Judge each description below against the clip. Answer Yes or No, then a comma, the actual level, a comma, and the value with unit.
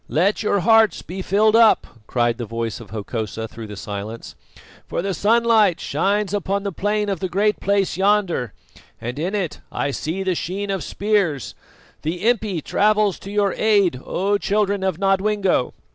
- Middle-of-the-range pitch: No, high, 195 Hz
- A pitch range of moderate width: Yes, average, 5.0 semitones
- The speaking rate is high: No, average, 170 wpm